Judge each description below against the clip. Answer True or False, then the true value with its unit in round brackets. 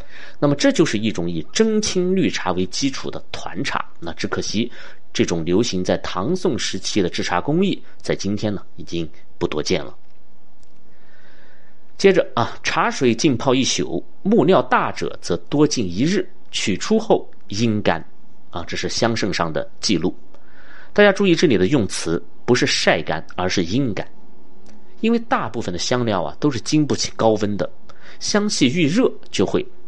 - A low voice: True (115 Hz)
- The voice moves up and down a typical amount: False (8.4 semitones)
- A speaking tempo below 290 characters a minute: True (235 characters per minute)